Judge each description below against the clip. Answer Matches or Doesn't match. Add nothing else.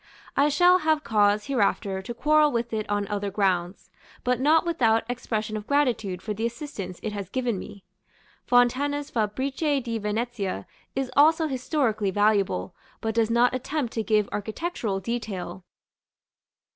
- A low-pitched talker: Doesn't match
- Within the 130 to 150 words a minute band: Matches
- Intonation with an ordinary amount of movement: Matches